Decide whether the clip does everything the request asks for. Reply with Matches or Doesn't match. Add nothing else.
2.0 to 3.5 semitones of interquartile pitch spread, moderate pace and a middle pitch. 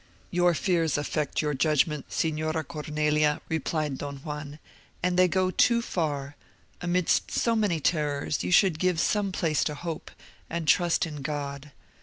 Matches